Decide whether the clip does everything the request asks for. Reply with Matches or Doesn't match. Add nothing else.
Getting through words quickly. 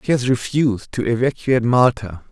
Doesn't match